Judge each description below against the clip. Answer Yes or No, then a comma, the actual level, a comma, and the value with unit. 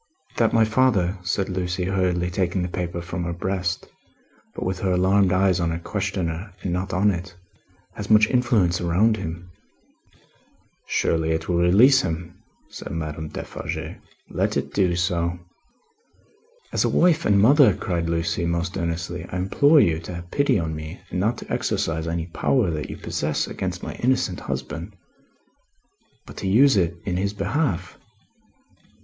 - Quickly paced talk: No, average, 160 wpm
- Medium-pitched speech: No, very low, 90 Hz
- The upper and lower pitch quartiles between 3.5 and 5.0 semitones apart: No, average, 2.9 semitones